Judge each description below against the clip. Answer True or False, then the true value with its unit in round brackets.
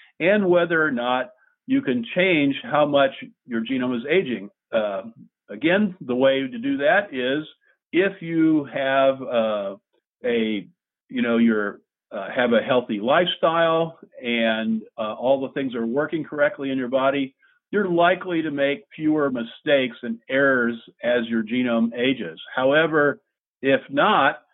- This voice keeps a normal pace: True (145 wpm)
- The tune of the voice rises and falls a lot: True (6.2 semitones)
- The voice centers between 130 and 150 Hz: True (140 Hz)